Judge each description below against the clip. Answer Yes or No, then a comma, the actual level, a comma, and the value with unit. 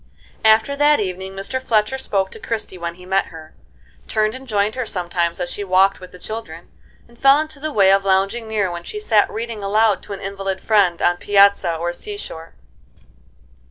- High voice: Yes, high, 200 Hz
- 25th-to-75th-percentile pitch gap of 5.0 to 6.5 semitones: No, average, 3.5 semitones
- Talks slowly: No, average, 195 wpm